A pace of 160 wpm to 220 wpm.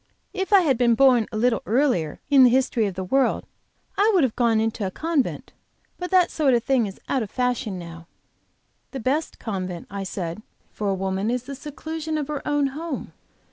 Yes: fast, 205 wpm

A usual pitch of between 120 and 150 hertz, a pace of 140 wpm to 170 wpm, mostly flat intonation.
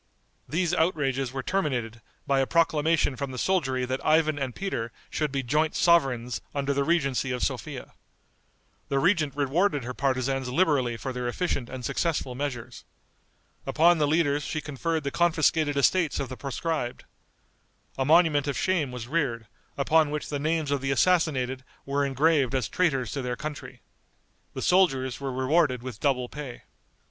No: medium, 140 Hz; average, 160 wpm; average, 3.6 semitones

